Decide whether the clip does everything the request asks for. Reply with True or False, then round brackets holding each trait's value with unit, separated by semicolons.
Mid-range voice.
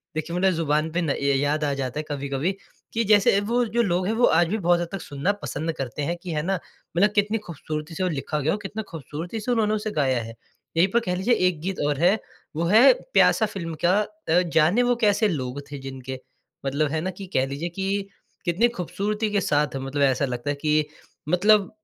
True (170 Hz)